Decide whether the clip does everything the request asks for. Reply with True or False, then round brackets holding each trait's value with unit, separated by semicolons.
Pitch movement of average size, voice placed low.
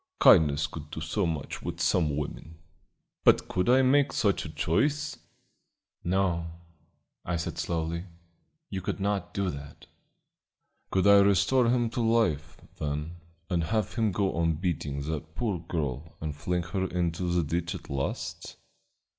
True (4.0 semitones; 85 Hz)